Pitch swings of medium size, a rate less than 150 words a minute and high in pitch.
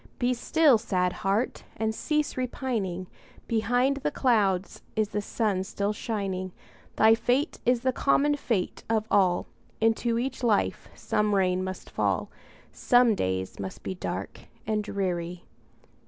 Yes: average, 4.6 semitones; average, 140 wpm; high, 215 Hz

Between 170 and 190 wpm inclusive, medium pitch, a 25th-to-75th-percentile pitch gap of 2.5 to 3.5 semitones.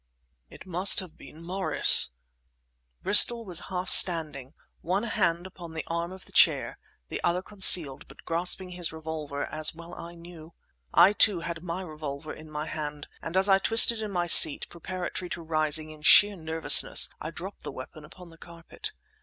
Yes: average, 175 wpm; medium, 170 Hz; average, 2.9 semitones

